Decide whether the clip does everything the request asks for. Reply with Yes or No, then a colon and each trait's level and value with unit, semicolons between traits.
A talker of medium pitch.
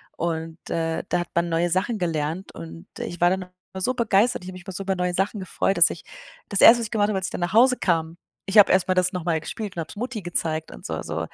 Yes: medium, 180 Hz